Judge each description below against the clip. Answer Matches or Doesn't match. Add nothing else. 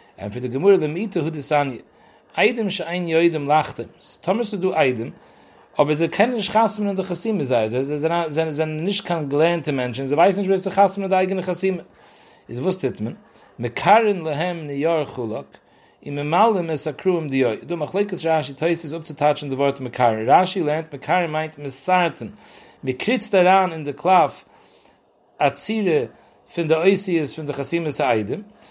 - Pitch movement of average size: Matches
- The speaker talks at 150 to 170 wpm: Doesn't match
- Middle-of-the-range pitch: Matches